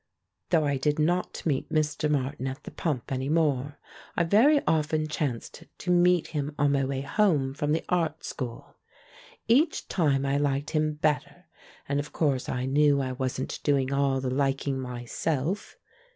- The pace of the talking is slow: No, average, 165 wpm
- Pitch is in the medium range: Yes, medium, 145 Hz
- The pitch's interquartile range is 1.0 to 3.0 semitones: Yes, average, 2.7 semitones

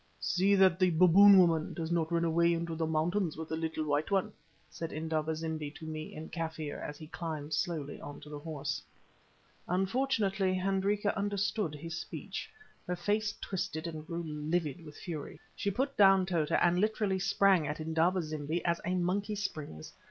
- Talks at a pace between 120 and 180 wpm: Yes, average, 175 wpm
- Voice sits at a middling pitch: Yes, medium, 170 Hz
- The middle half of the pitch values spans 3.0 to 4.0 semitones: Yes, average, 3.4 semitones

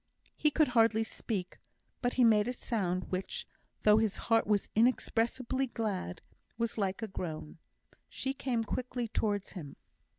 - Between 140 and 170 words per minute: Yes, average, 145 wpm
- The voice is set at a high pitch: Yes, high, 225 Hz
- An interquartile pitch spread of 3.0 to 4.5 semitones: Yes, average, 3.8 semitones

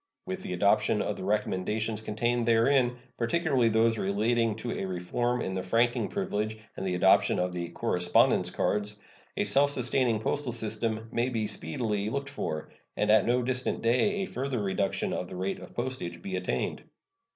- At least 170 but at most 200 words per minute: Yes, average, 175 wpm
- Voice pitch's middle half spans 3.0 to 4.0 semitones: Yes, average, 3.6 semitones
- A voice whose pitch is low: Yes, low, 115 Hz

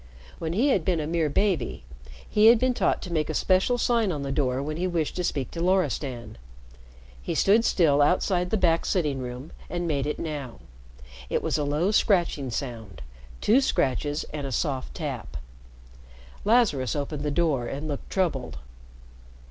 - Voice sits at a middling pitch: Yes, medium, 155 Hz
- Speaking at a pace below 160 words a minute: No, average, 175 wpm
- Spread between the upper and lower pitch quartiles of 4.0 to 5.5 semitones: Yes, average, 5.0 semitones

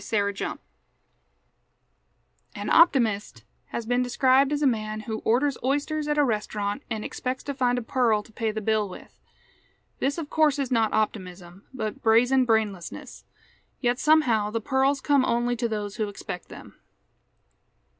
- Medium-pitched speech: No, high, 235 Hz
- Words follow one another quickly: No, average, 160 wpm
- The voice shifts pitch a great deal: No, average, 3.9 semitones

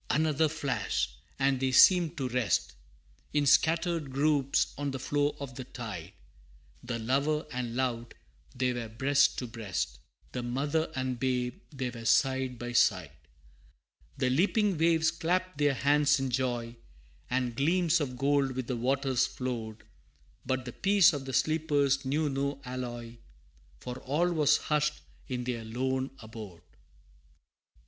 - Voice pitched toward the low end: Yes, low, 130 Hz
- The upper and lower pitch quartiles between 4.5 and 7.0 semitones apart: No, average, 3.2 semitones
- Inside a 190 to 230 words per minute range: No, average, 145 wpm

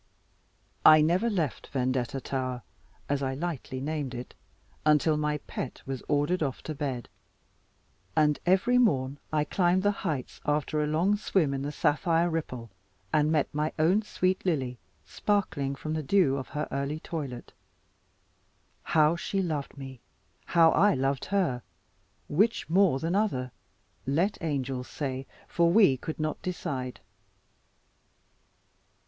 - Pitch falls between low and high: Yes, medium, 150 Hz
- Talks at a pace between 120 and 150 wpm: Yes, average, 140 wpm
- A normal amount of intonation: Yes, average, 4.3 semitones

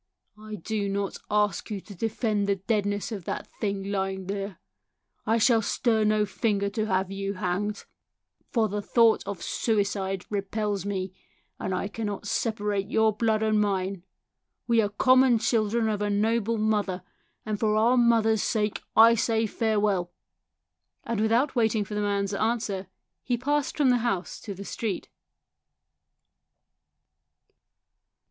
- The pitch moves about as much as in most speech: No, narrow, 2.0 semitones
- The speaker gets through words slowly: No, average, 145 wpm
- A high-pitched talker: Yes, high, 210 Hz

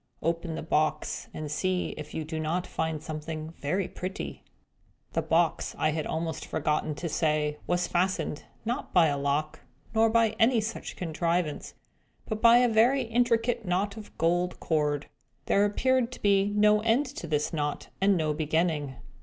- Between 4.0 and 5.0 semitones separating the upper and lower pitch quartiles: No, wide, 5.4 semitones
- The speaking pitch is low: No, medium, 175 Hz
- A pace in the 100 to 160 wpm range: No, average, 170 wpm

